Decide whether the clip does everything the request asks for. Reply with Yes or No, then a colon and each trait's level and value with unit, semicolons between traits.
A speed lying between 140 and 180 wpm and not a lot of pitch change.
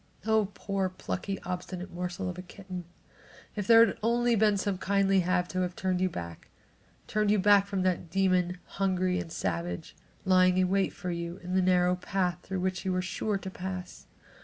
No: average, 190 wpm; narrow, 1.5 semitones